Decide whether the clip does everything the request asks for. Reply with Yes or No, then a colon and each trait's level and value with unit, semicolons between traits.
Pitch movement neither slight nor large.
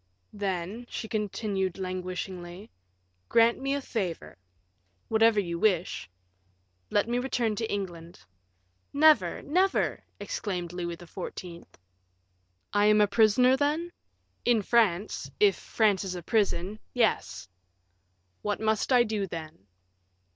Yes: average, 4.4 semitones